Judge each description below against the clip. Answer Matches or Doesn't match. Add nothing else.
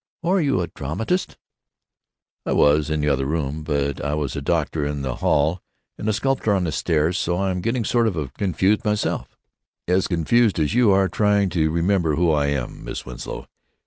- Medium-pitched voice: Doesn't match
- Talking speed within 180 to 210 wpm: Matches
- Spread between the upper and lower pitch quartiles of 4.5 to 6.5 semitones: Matches